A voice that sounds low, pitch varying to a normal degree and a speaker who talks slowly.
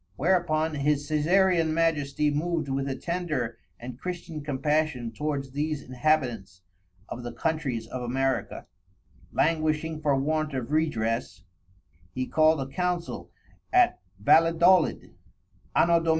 No: medium, 150 Hz; average, 3.4 semitones; slow, 120 wpm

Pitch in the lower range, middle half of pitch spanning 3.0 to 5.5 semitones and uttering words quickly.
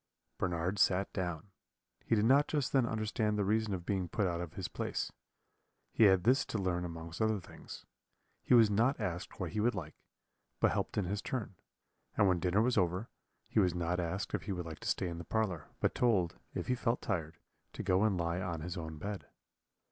Yes: very low, 95 Hz; average, 3.9 semitones; fast, 215 wpm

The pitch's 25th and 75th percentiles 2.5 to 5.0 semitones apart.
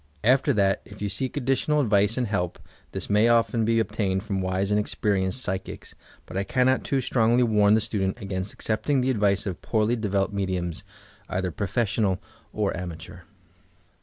Yes: average, 3.4 semitones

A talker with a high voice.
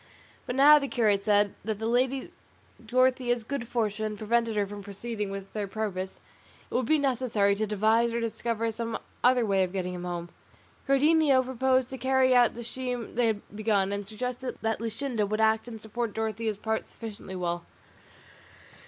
Yes: high, 225 Hz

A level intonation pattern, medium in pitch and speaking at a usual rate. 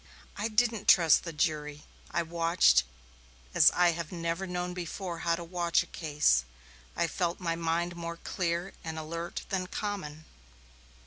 Yes: narrow, 1.6 semitones; medium, 170 Hz; average, 150 wpm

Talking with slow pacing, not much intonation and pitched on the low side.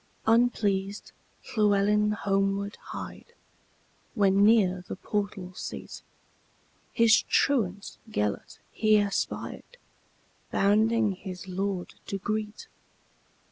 No: slow, 70 wpm; narrow, 1.8 semitones; high, 205 Hz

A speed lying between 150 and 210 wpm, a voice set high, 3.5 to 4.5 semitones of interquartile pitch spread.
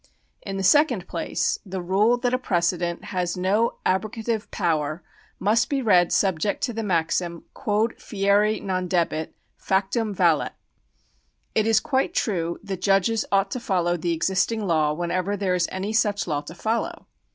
Yes: average, 165 wpm; high, 195 Hz; average, 3.8 semitones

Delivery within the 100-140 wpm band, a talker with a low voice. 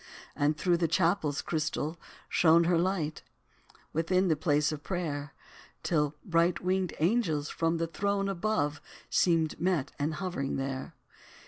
No: slow, 135 wpm; medium, 165 Hz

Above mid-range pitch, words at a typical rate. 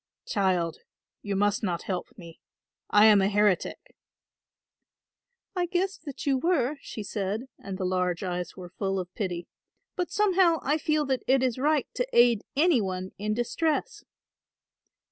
Yes: high, 215 Hz; average, 155 wpm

